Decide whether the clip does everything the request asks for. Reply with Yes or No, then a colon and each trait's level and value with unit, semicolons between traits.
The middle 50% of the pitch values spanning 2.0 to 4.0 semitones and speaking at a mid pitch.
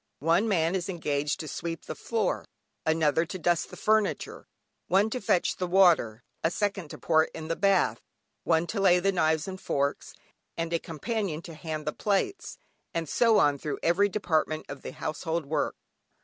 Yes: average, 3.7 semitones; medium, 170 Hz